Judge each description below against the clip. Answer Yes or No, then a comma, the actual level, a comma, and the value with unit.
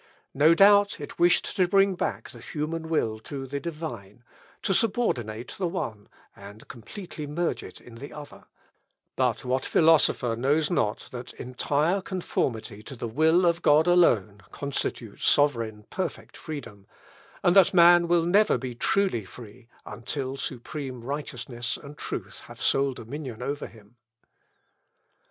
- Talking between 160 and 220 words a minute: No, average, 140 wpm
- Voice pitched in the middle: Yes, medium, 145 Hz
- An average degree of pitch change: No, wide, 6.3 semitones